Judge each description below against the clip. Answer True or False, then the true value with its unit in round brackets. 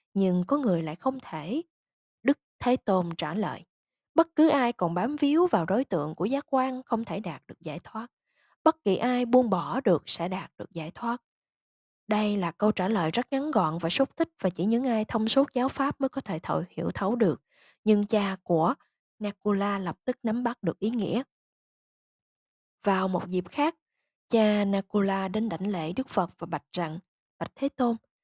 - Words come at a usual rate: True (200 wpm)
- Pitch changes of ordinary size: False (5.9 semitones)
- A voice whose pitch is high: True (215 Hz)